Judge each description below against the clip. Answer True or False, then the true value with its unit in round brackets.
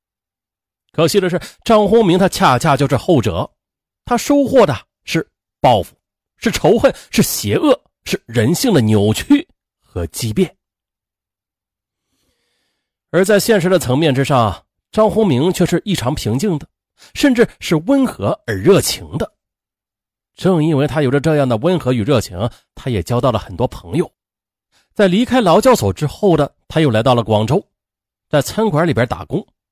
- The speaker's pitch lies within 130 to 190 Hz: True (140 Hz)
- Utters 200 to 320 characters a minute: True (220 characters per minute)